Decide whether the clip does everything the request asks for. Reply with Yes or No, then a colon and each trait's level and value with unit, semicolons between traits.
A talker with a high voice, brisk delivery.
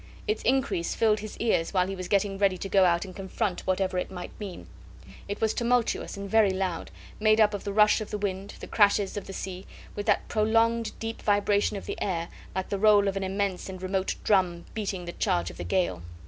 Yes: high, 200 Hz; fast, 225 wpm